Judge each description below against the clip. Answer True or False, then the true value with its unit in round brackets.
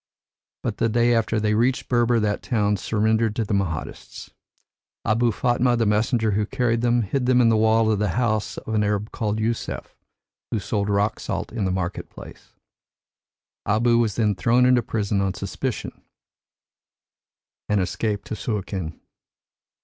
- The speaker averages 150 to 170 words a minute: True (160 wpm)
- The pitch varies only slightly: True (2.3 semitones)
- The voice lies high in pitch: False (110 Hz)